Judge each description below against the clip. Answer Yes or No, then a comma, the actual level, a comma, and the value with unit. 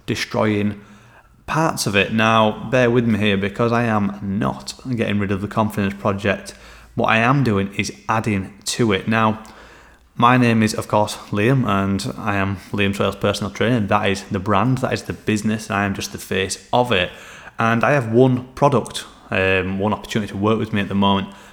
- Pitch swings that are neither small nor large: No, narrow, 2.3 semitones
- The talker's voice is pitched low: Yes, low, 105 Hz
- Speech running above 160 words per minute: Yes, average, 200 wpm